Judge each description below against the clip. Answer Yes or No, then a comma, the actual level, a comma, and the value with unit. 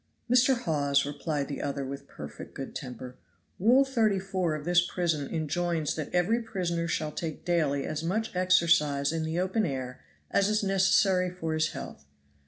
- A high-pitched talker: No, medium, 170 Hz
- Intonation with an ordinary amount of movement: Yes, average, 4.3 semitones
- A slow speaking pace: No, average, 165 wpm